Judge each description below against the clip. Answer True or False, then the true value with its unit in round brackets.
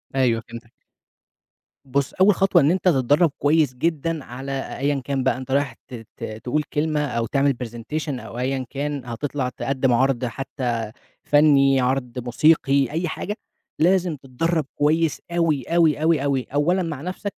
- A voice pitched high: False (140 Hz)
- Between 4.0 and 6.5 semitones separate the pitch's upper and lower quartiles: False (3.5 semitones)